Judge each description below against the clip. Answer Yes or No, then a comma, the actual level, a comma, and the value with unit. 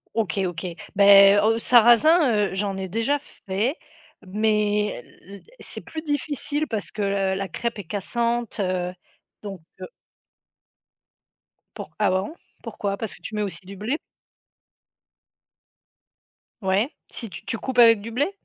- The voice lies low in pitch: No, high, 210 Hz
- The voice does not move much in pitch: No, average, 3.2 semitones